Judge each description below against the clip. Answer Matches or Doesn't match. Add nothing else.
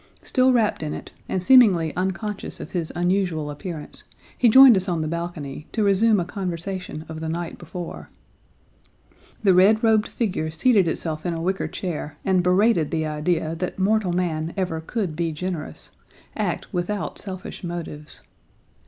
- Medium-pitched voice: Matches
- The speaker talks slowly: Doesn't match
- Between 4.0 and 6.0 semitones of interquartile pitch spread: Doesn't match